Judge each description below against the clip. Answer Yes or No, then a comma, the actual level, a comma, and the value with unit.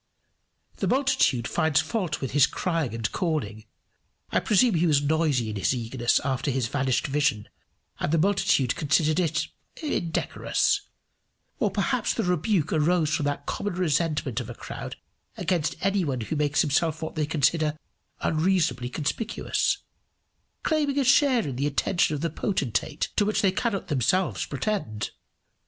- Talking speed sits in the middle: Yes, average, 155 wpm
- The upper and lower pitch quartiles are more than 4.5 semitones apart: Yes, average, 5.2 semitones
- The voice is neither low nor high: Yes, medium, 155 Hz